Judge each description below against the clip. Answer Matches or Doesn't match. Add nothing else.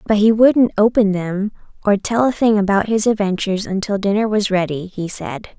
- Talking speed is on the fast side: Doesn't match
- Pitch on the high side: Matches